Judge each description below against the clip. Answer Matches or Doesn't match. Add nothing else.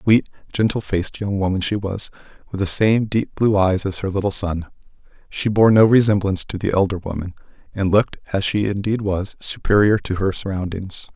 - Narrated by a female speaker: Doesn't match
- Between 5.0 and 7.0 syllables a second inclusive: Matches